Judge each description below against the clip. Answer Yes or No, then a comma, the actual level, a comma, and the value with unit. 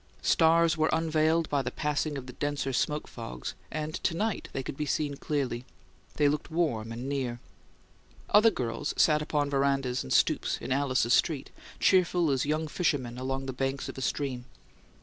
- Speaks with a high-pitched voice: No, medium, 145 Hz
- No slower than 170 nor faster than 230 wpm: Yes, average, 175 wpm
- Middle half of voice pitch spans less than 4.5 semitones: Yes, average, 3.2 semitones